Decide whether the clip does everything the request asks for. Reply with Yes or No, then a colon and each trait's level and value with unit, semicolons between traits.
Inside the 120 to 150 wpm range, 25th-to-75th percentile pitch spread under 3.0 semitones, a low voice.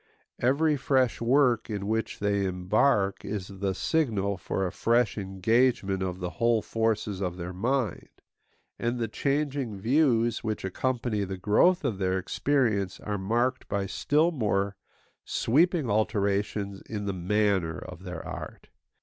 No: average, 140 wpm; average, 4.2 semitones; low, 105 Hz